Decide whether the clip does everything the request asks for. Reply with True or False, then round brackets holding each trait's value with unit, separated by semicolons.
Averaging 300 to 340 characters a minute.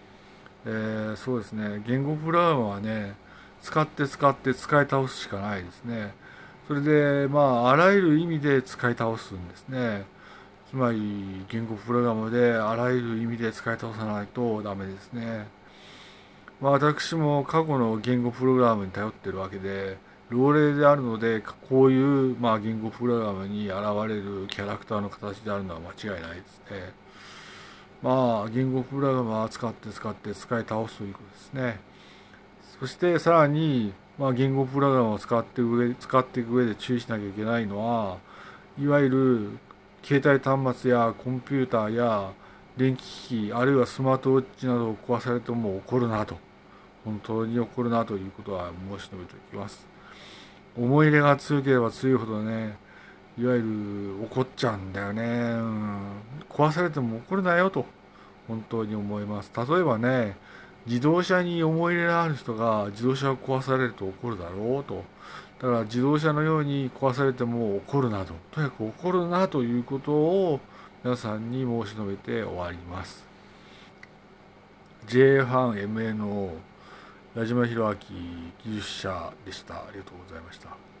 True (320 characters per minute)